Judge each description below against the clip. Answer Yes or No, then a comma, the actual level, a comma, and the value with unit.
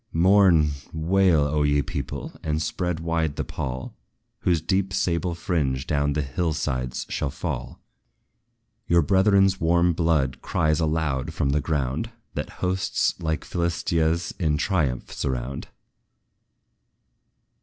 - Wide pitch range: No, average, 3.4 semitones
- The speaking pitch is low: Yes, very low, 80 Hz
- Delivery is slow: Yes, slow, 125 wpm